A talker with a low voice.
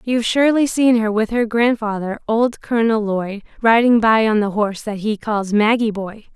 No: high, 220 Hz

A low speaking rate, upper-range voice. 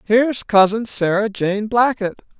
Yes: slow, 125 wpm; high, 215 Hz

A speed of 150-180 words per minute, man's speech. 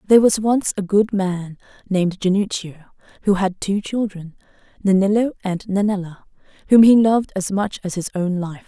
No: average, 165 wpm; female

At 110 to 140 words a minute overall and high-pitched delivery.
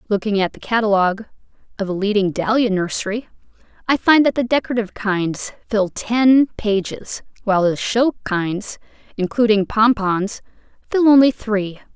Yes: slow, 135 wpm; high, 215 Hz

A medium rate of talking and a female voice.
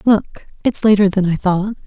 Yes: average, 195 wpm; female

